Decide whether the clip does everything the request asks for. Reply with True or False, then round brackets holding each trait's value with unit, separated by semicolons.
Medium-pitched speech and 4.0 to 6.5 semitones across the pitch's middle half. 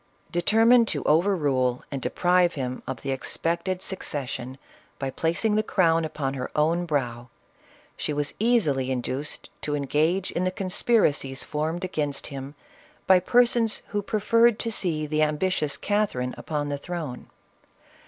True (155 Hz; 5.3 semitones)